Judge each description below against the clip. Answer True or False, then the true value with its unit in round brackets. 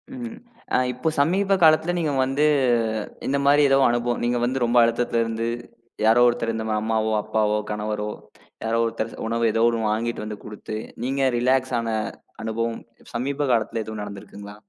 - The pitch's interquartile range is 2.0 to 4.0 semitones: True (3.3 semitones)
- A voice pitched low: True (115 Hz)